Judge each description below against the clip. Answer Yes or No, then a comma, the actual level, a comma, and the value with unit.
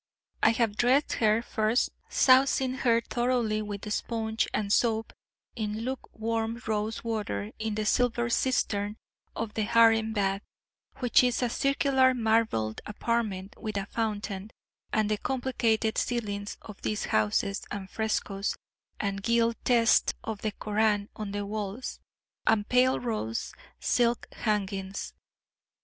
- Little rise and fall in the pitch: Yes, narrow, 2.3 semitones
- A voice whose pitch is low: No, high, 220 Hz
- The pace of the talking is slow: Yes, slow, 130 wpm